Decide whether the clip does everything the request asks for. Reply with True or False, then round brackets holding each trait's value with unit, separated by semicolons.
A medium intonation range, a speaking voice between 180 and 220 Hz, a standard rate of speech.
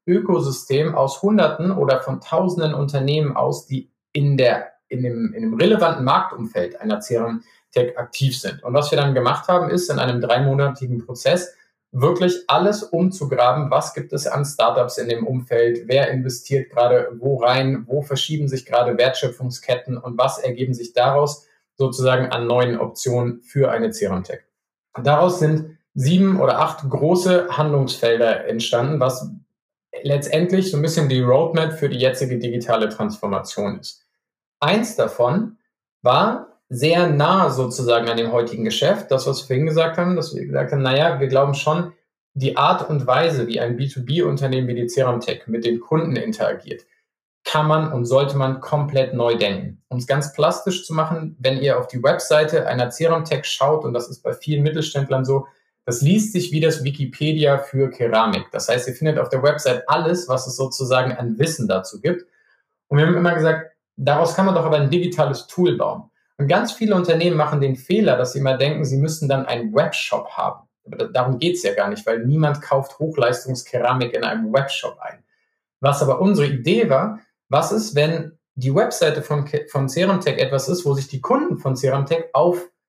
False (4.2 semitones; 140 Hz; 180 wpm)